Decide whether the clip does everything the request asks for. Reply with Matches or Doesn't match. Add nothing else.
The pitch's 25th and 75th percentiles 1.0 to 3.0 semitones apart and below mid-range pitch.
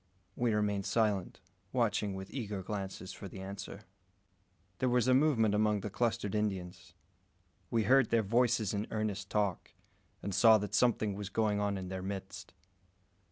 Matches